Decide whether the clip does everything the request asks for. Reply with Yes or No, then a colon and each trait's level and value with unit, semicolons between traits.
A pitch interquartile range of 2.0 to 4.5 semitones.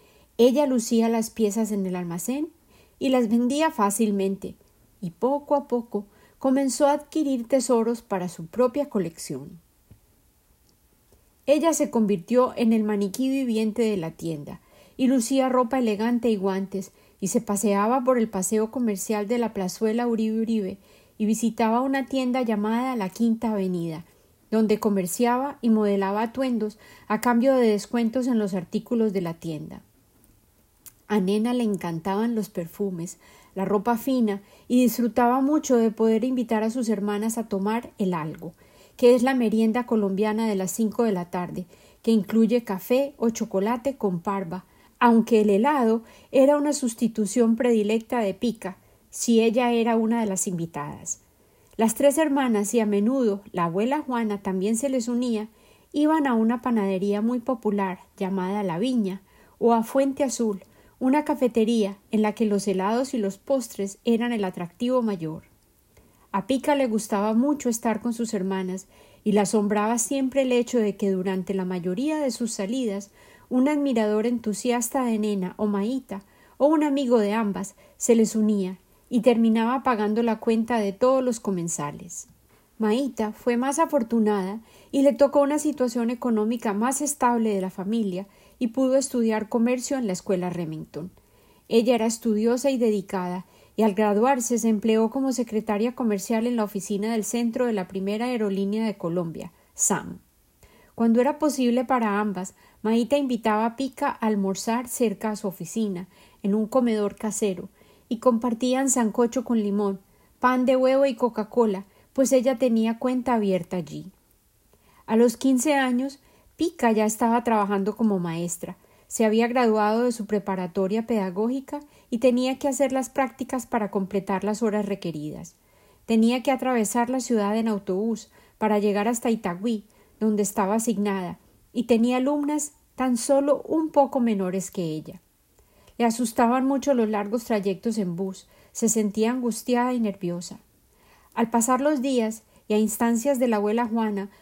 Yes: average, 3.6 semitones